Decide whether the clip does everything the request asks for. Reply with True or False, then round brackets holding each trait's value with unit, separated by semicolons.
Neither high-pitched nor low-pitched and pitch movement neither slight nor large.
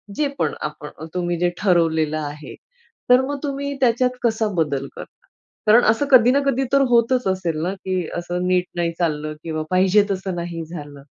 False (180 Hz; 6.4 semitones)